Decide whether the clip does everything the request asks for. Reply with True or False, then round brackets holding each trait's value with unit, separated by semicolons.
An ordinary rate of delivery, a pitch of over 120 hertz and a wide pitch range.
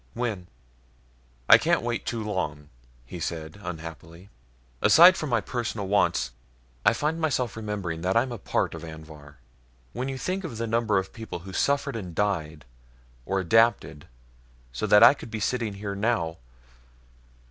False (160 wpm; 105 Hz; 6.0 semitones)